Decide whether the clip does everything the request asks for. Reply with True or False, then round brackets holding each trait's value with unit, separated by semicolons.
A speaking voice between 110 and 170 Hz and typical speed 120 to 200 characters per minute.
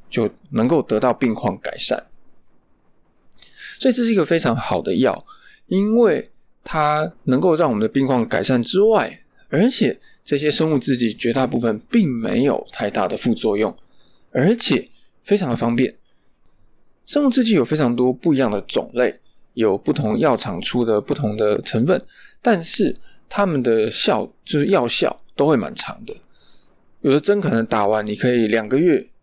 False (135 Hz; 240 characters per minute)